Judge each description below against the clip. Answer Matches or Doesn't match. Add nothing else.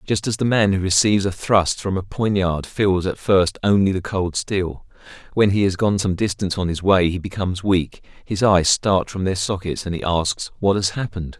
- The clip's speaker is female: Doesn't match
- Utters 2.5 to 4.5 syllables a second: Doesn't match